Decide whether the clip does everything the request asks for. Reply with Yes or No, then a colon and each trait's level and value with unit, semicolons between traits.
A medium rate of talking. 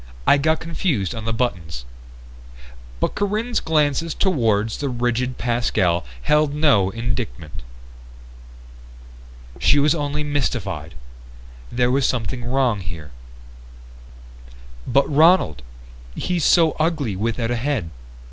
No: slow, 110 wpm